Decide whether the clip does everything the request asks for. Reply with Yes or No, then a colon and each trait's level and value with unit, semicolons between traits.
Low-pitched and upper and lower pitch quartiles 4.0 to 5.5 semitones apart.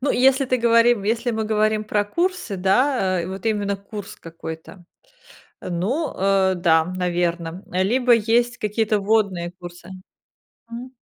No: high, 205 Hz; average, 4.4 semitones